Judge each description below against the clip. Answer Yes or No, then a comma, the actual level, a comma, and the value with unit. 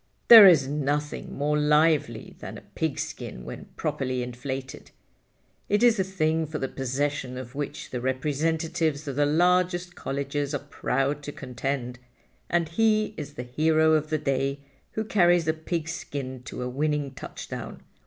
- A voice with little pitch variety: No, average, 3.2 semitones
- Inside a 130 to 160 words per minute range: Yes, average, 155 wpm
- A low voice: No, medium, 150 Hz